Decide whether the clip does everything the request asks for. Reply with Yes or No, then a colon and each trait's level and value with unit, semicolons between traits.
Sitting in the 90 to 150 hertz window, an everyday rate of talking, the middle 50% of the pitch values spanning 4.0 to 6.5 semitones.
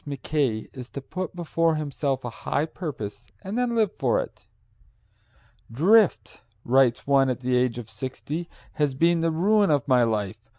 Yes: medium, 140 Hz; average, 165 wpm; average, 4.9 semitones